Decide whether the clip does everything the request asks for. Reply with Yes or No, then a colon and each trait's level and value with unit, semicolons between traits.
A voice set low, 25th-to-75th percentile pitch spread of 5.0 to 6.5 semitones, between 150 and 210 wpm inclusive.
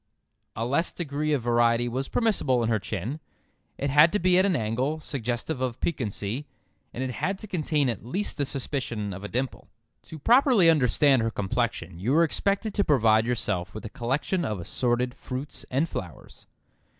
Yes: low, 130 Hz; average, 5.3 semitones; average, 180 wpm